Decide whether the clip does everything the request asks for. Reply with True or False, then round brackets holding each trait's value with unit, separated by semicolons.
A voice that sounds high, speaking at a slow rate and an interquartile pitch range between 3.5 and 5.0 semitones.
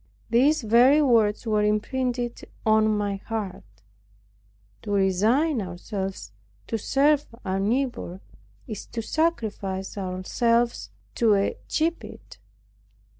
True (220 Hz; 100 wpm; 4.0 semitones)